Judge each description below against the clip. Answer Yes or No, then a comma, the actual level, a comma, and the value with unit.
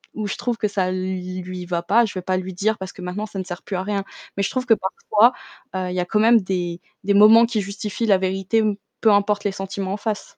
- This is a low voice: No, high, 195 Hz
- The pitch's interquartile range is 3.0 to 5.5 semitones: No, narrow, 2.4 semitones